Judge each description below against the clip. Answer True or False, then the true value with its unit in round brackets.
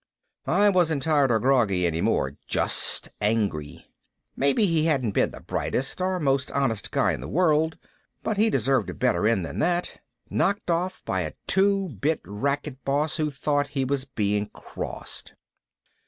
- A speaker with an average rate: True (165 wpm)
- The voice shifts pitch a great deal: True (6.3 semitones)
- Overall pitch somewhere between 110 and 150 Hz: True (140 Hz)